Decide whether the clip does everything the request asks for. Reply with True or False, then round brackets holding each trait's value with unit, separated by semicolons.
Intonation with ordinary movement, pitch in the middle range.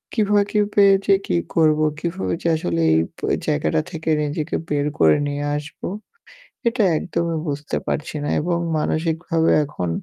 True (3.2 semitones; 160 Hz)